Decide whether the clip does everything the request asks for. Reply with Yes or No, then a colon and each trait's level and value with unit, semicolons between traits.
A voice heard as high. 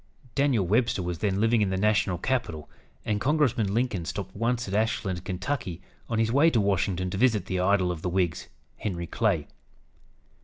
No: low, 100 Hz